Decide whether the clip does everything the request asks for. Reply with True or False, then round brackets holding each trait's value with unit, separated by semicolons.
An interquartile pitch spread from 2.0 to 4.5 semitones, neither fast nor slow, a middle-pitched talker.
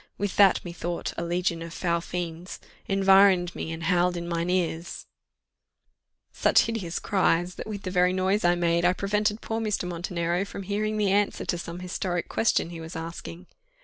True (2.5 semitones; 180 wpm; 180 Hz)